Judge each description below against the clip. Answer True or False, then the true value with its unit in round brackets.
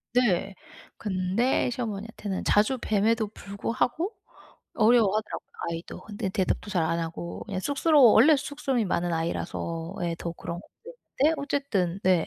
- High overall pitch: True (210 Hz)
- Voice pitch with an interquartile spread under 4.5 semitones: False (5.5 semitones)